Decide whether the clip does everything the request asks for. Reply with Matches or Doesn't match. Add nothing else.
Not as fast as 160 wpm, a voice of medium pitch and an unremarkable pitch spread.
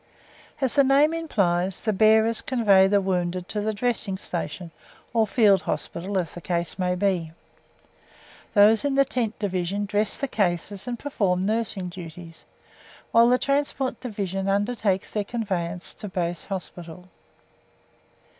Doesn't match